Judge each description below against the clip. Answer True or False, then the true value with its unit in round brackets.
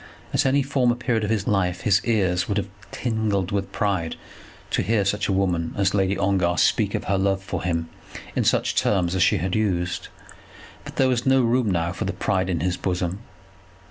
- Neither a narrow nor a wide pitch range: True (3.2 semitones)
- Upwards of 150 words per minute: True (200 wpm)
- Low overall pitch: True (95 Hz)